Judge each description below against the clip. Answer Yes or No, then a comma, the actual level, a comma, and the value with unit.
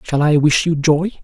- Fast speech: Yes, fast, 245 wpm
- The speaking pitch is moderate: Yes, medium, 155 Hz